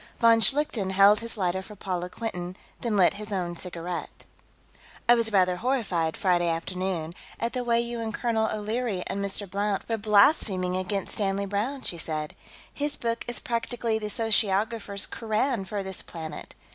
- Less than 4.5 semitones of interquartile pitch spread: Yes, average, 3.9 semitones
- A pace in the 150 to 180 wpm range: Yes, average, 165 wpm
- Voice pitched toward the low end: No, high, 205 Hz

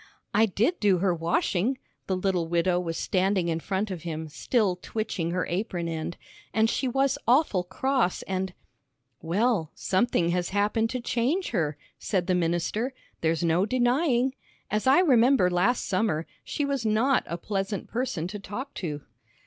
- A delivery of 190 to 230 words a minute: No, average, 165 wpm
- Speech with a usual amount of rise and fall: No, wide, 5.7 semitones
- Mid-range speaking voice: No, high, 195 Hz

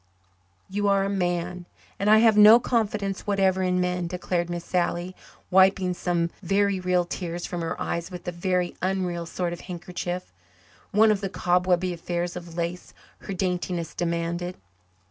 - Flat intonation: Yes, narrow, 1.8 semitones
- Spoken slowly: No, average, 160 wpm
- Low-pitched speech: No, medium, 180 Hz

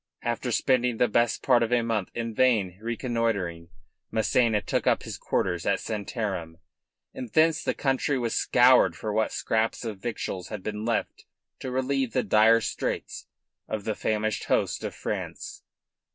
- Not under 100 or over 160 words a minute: Yes, average, 155 wpm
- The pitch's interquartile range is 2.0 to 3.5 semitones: Yes, narrow, 2.5 semitones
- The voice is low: Yes, low, 115 Hz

